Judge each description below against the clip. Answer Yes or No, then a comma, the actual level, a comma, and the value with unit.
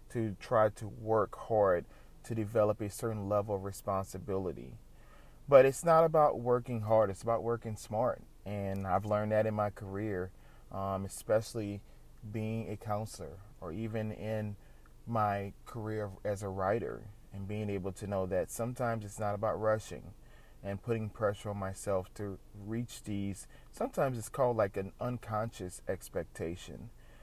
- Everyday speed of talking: Yes, average, 150 wpm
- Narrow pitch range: Yes, narrow, 2.2 semitones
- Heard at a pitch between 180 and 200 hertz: No, low, 105 Hz